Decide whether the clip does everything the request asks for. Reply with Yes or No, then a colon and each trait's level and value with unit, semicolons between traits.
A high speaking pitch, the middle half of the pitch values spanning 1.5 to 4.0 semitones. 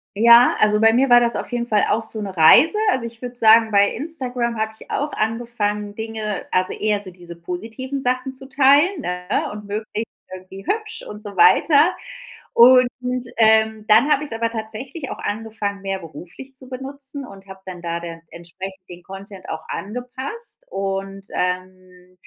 No: high, 220 Hz; average, 4.5 semitones